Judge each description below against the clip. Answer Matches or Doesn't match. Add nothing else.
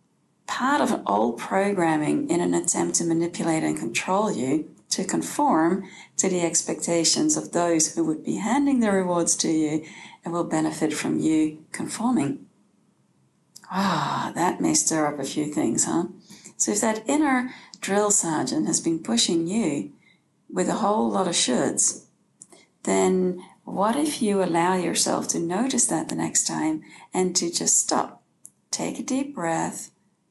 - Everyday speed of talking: Matches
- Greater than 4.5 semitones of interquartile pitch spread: Matches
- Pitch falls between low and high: Matches